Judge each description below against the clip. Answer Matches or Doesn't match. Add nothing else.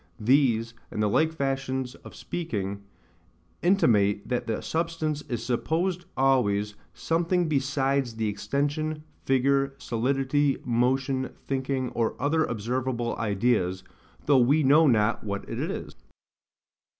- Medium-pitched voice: Doesn't match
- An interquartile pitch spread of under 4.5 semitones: Matches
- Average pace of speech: Doesn't match